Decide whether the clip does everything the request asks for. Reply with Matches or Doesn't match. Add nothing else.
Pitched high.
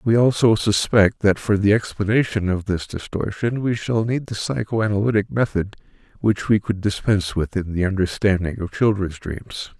Doesn't match